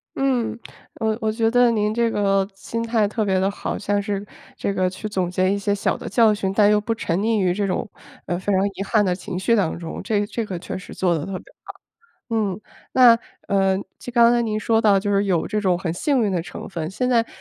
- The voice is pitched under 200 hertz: No, high, 205 Hz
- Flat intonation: No, average, 3.0 semitones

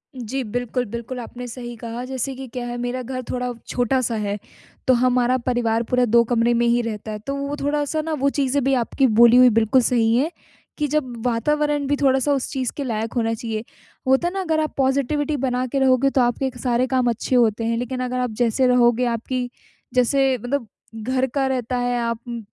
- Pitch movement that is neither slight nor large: No, narrow, 2.1 semitones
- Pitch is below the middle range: No, very high, 250 Hz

